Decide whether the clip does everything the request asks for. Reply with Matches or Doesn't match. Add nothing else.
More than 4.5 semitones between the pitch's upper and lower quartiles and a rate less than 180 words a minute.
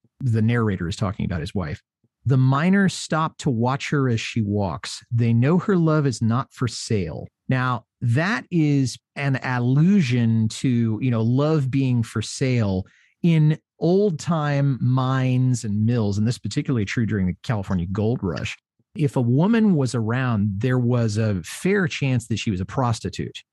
Doesn't match